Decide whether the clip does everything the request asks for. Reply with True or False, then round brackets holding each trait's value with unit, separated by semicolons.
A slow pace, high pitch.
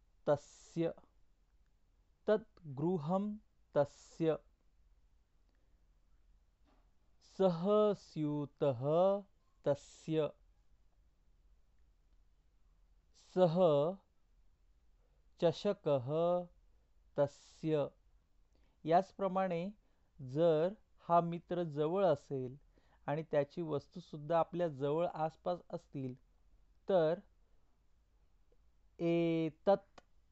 False (50 wpm; 145 Hz)